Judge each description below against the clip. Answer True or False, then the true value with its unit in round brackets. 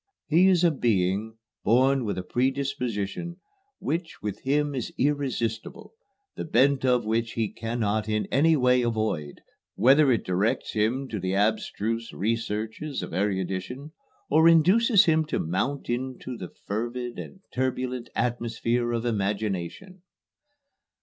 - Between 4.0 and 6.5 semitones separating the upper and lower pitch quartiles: True (4.5 semitones)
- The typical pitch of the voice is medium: False (120 Hz)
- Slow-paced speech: True (130 wpm)